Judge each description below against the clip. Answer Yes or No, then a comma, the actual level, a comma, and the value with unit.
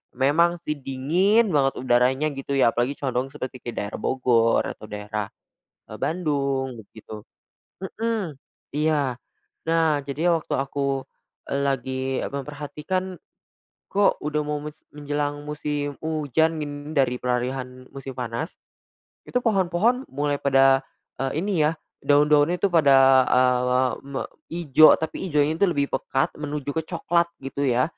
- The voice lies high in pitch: No, medium, 145 Hz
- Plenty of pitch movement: No, average, 3.2 semitones